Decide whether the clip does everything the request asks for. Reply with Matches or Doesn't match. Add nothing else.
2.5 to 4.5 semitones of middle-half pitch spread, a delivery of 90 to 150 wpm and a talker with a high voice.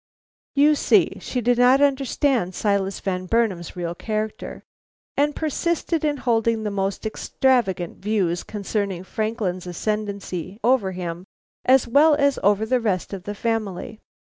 Doesn't match